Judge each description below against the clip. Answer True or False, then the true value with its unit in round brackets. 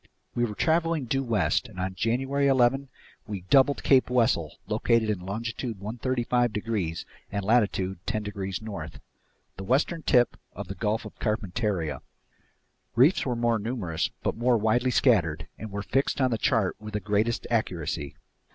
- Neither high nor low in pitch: False (115 Hz)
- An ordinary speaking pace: True (160 wpm)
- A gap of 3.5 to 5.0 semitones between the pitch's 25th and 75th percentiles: True (3.9 semitones)